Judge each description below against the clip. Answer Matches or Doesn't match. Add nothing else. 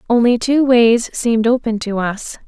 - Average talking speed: Matches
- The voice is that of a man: Doesn't match